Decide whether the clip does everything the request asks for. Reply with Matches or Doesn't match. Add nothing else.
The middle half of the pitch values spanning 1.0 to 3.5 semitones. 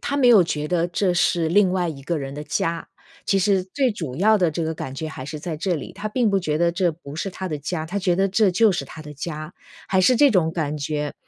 Doesn't match